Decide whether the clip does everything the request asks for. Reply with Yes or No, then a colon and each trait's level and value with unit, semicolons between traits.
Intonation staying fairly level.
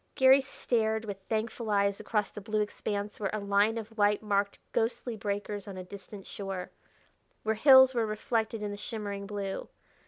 Yes: narrow, 1.8 semitones